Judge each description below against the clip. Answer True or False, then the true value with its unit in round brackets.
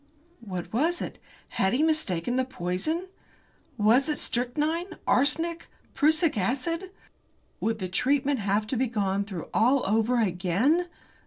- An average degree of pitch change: False (7.3 semitones)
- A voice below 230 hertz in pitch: False (250 Hz)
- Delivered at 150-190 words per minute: False (135 wpm)